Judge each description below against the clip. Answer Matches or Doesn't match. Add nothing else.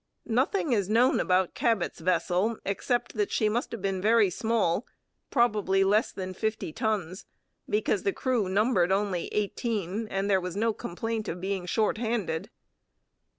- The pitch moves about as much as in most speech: Matches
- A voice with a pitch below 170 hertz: Doesn't match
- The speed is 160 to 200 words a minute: Doesn't match